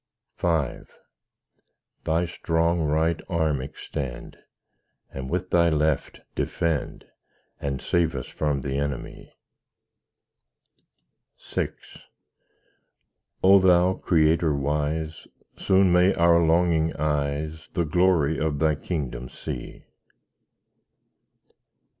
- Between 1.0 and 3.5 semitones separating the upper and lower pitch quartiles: Yes, average, 2.8 semitones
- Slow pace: Yes, slow, 90 wpm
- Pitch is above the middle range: No, very low, 80 Hz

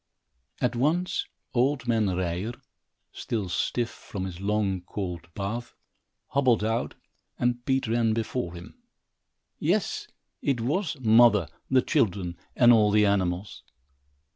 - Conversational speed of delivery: No, slow, 120 wpm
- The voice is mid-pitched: No, low, 110 Hz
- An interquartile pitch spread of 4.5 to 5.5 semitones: No, average, 4.1 semitones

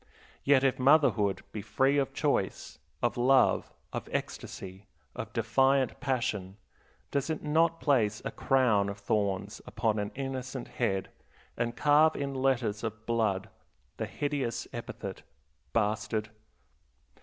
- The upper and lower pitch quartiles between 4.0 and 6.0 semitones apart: Yes, average, 4.5 semitones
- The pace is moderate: No, slow, 125 wpm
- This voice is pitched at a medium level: No, low, 120 Hz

